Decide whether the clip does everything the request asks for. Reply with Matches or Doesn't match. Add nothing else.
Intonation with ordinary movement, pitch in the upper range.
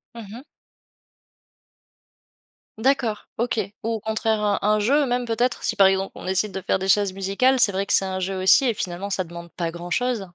Matches